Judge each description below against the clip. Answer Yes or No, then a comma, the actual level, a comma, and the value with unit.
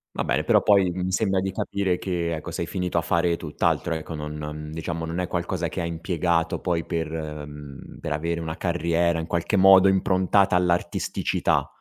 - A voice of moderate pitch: No, very low, 85 Hz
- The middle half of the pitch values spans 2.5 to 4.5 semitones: No, narrow, 2.1 semitones